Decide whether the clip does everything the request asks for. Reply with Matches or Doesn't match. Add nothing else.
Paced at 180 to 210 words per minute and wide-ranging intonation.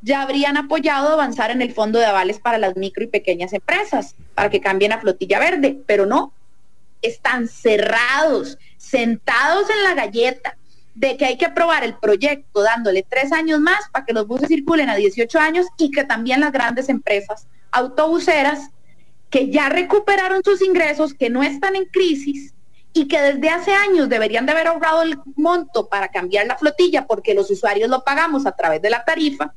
Matches